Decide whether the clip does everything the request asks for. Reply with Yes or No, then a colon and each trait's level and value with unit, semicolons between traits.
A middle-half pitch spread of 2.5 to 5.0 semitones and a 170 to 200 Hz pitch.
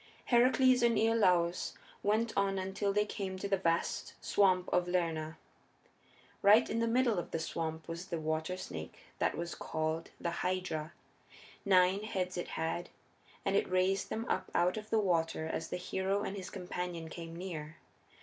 Yes: average, 3.2 semitones; medium, 185 Hz